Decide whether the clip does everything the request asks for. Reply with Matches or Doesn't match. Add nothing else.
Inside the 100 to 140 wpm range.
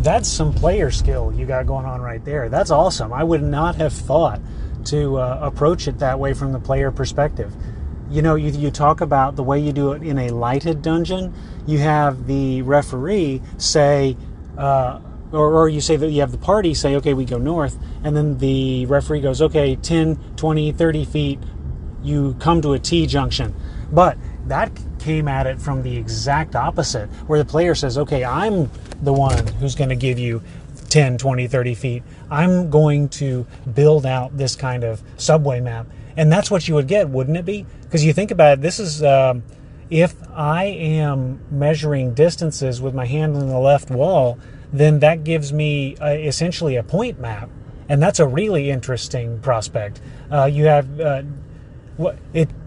Doesn't match